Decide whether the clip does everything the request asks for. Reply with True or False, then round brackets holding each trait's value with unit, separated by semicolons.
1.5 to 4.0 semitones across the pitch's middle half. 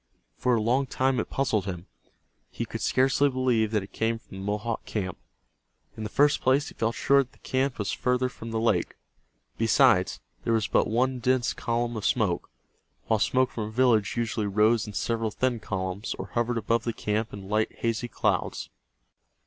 True (3.0 semitones)